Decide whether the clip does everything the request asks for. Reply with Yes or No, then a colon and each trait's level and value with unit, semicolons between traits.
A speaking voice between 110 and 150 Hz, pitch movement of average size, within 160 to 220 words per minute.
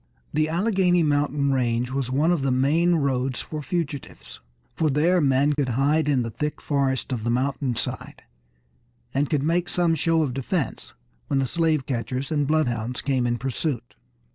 Yes: medium, 140 Hz; average, 3.4 semitones; average, 165 wpm